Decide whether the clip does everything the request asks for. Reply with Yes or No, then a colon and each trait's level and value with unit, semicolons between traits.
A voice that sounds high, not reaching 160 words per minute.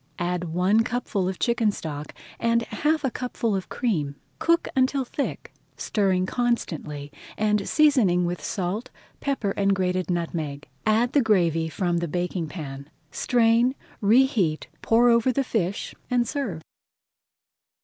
Yes: high, 200 Hz; slow, 135 wpm